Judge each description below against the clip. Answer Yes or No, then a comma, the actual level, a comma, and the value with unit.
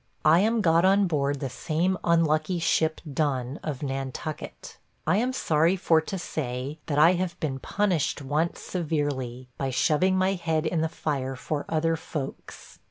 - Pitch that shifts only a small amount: No, average, 3.4 semitones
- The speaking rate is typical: Yes, average, 165 wpm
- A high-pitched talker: No, medium, 155 Hz